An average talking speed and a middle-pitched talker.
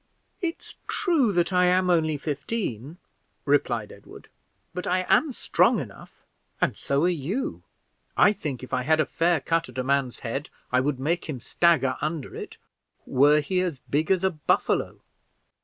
Yes: average, 170 wpm; medium, 155 Hz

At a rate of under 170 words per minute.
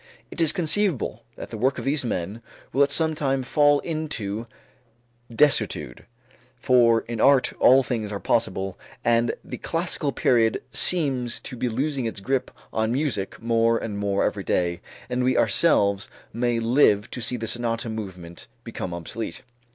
Yes: average, 160 wpm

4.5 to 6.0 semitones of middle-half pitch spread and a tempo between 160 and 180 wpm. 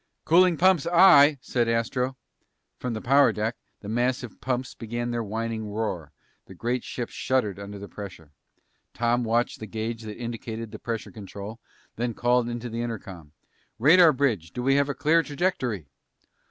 No: average, 3.1 semitones; average, 165 wpm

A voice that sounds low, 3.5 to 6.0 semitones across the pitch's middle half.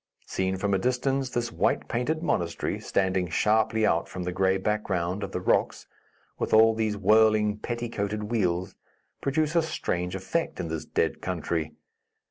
Yes: low, 105 Hz; average, 4.3 semitones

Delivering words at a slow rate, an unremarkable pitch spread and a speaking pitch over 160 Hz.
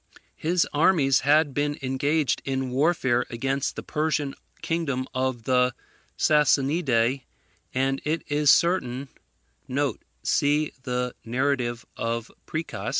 No: slow, 105 wpm; average, 3.1 semitones; low, 135 Hz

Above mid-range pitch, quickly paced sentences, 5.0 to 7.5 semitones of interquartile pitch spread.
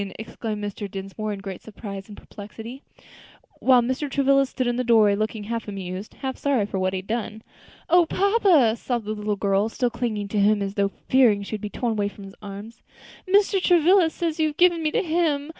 Yes: high, 225 Hz; fast, 210 wpm; average, 5.3 semitones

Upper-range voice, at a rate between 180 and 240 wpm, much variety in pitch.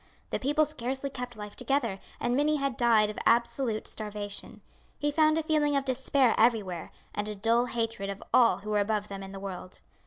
No: high, 230 Hz; average, 195 wpm; average, 4.8 semitones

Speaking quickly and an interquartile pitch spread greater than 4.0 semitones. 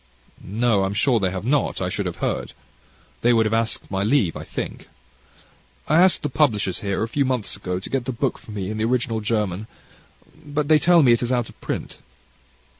Yes: fast, 215 wpm; average, 4.4 semitones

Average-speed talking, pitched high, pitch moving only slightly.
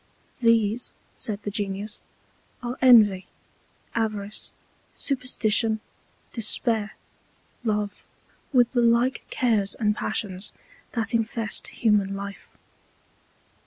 No: slow, 90 wpm; high, 220 Hz; narrow, 2.3 semitones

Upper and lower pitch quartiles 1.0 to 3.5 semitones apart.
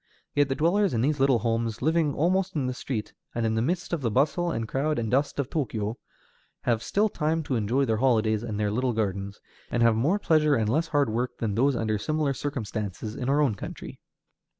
No: average, 5.3 semitones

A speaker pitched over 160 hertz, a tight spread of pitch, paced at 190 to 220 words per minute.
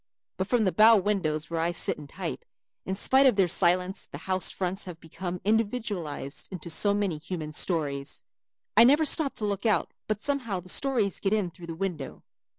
No: high, 190 Hz; average, 4.2 semitones; average, 195 wpm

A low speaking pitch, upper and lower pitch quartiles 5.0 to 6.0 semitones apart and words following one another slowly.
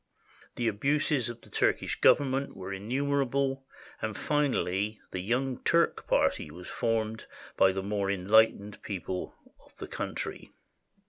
Yes: low, 110 Hz; wide, 5.4 semitones; slow, 130 wpm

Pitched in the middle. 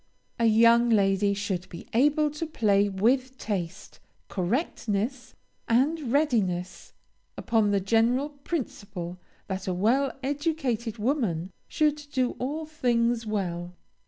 No: high, 230 Hz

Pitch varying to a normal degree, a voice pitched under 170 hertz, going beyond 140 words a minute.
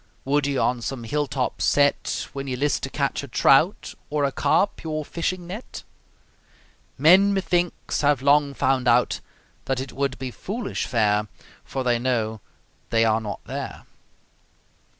Yes: average, 3.4 semitones; low, 135 Hz; average, 155 wpm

